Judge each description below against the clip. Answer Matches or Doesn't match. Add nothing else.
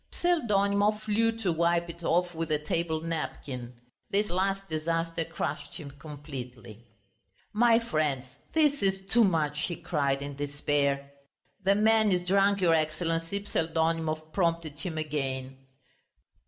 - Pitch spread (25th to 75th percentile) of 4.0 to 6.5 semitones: Matches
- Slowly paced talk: Matches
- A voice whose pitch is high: Doesn't match